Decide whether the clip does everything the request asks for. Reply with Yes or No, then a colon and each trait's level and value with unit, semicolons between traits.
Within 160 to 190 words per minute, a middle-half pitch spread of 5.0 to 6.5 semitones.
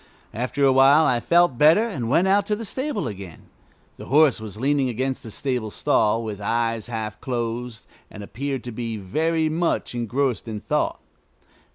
Yes: average, 175 wpm; average, 5.3 semitones